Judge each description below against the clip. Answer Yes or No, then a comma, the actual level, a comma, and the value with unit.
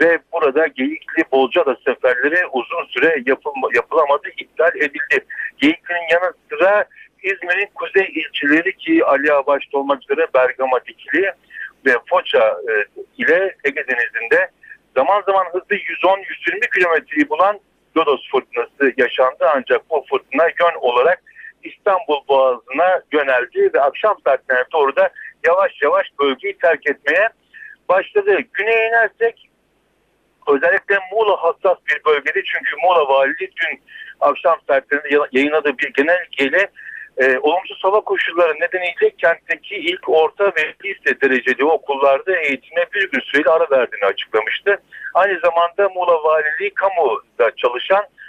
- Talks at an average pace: Yes, average, 125 wpm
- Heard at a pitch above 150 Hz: Yes, high, 190 Hz